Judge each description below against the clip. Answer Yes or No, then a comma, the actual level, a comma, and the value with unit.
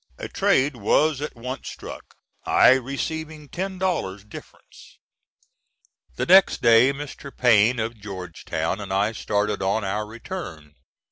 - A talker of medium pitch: No, low, 115 Hz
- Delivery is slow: Yes, slow, 130 wpm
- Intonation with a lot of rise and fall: Yes, wide, 6.2 semitones